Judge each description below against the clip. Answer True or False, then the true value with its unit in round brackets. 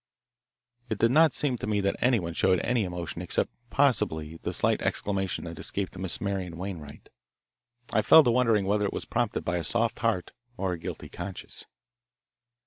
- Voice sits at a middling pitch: False (100 Hz)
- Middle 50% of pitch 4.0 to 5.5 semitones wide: True (4.6 semitones)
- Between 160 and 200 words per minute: True (175 wpm)